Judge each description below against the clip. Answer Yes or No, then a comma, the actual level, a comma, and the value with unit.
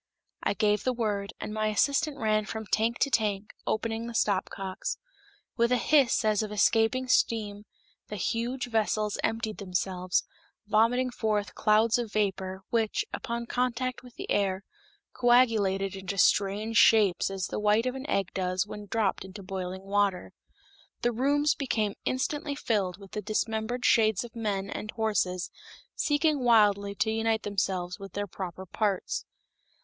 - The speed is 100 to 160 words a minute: Yes, average, 150 wpm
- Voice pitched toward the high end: Yes, high, 215 Hz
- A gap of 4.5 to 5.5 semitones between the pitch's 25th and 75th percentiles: No, average, 3.0 semitones